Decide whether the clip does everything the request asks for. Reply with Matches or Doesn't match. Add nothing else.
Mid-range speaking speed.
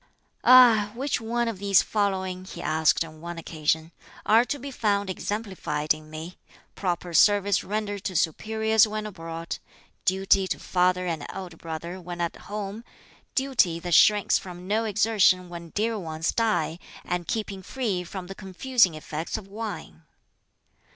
Matches